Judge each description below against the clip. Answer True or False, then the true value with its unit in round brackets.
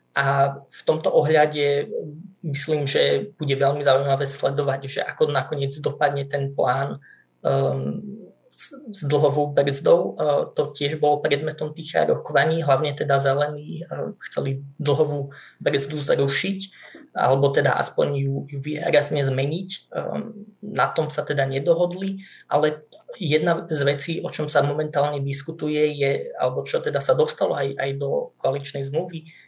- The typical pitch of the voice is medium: True (145 Hz)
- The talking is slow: False (140 wpm)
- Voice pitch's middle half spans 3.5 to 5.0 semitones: False (2.7 semitones)